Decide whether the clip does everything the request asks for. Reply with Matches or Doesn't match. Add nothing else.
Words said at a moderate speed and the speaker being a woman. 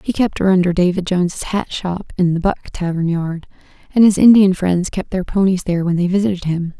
Doesn't match